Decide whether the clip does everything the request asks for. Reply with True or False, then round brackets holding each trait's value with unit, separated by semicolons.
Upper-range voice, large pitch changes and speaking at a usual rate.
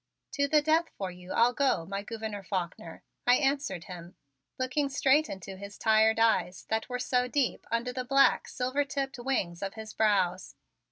True (230 Hz; 5.7 semitones; 175 wpm)